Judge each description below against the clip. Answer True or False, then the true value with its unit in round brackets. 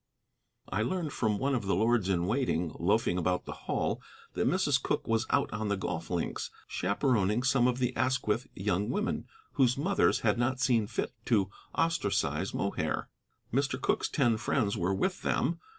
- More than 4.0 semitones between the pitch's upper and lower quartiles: True (4.7 semitones)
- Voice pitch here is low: True (115 Hz)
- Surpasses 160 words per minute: True (170 wpm)